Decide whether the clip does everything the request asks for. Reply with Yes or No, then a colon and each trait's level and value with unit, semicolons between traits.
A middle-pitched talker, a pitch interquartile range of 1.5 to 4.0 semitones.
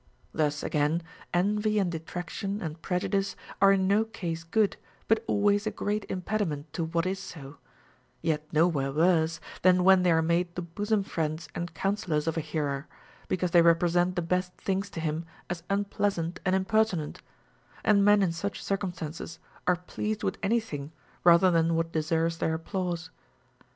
Yes: medium, 175 Hz; average, 3.3 semitones